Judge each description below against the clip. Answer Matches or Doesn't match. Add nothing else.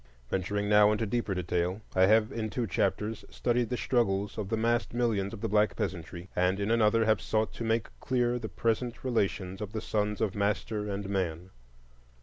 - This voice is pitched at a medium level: Doesn't match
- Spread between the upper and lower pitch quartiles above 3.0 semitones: Doesn't match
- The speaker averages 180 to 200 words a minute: Matches